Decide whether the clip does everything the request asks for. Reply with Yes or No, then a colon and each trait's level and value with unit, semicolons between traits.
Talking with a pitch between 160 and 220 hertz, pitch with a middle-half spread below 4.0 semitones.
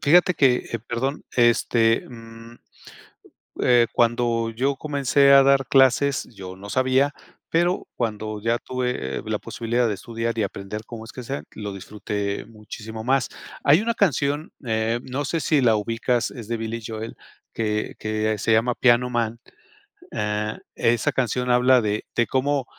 No: low, 120 Hz; average, 3.0 semitones